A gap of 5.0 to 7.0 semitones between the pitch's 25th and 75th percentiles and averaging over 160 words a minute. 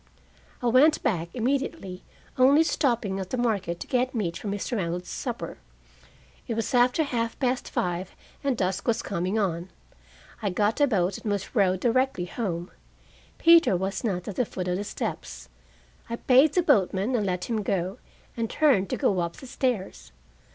Yes: wide, 5.4 semitones; average, 175 wpm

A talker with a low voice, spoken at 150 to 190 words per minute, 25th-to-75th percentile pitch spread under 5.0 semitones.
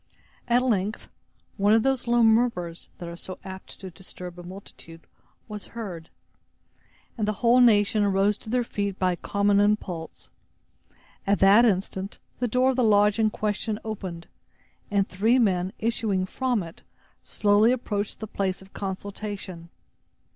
No: high, 205 Hz; average, 155 wpm; average, 2.9 semitones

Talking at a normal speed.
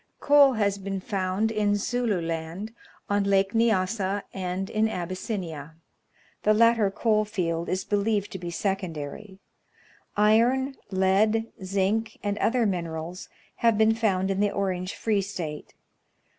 No: slow, 130 wpm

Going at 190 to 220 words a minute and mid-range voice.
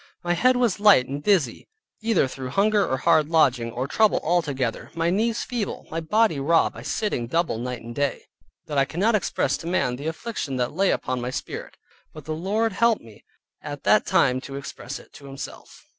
Yes: fast, 205 wpm; medium, 155 Hz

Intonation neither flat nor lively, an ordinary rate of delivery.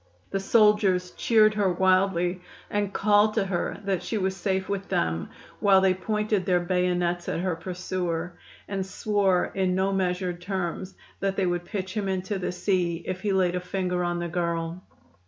No: narrow, 1.7 semitones; average, 175 wpm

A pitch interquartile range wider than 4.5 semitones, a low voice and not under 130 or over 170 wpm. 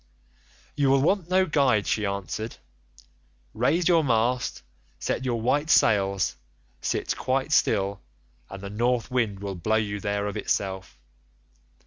Yes: average, 5.1 semitones; low, 110 Hz; slow, 135 wpm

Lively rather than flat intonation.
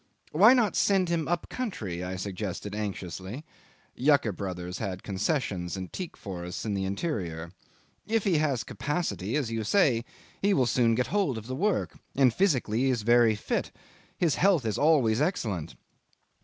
Yes: wide, 8.7 semitones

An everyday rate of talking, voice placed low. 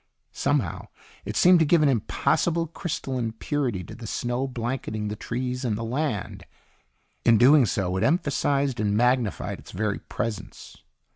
Yes: average, 150 wpm; low, 125 Hz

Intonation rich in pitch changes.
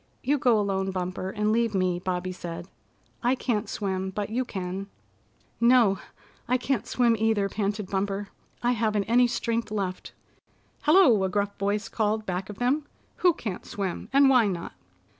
No: average, 3.6 semitones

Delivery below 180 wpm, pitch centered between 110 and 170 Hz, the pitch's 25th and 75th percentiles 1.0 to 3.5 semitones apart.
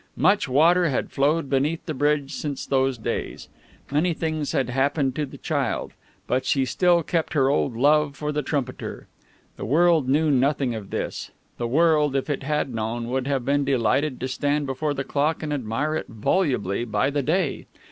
No: average, 185 wpm; medium, 140 Hz; average, 2.7 semitones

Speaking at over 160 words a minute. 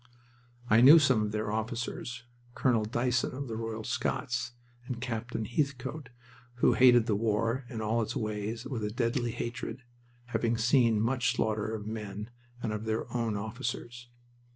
No: average, 155 wpm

